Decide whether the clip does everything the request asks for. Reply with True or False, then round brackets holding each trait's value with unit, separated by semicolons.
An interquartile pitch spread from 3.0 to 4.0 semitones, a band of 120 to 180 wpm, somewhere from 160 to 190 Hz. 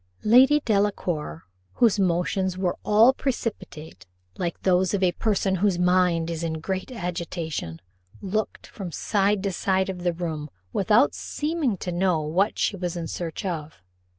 True (3.3 semitones; 150 wpm; 185 Hz)